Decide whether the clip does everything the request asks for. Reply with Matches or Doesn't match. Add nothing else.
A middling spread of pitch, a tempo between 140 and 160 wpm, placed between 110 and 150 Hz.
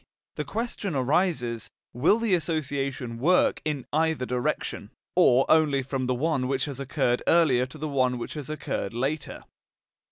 Matches